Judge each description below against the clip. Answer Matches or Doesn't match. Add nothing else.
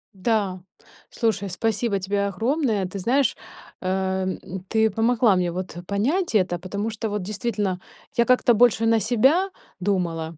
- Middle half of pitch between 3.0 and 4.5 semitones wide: Matches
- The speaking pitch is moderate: Doesn't match